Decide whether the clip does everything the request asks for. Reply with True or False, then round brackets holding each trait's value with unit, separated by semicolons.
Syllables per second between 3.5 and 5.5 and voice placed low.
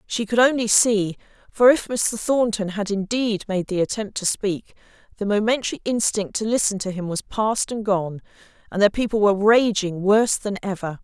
False (5.0 syllables/s; 210 Hz)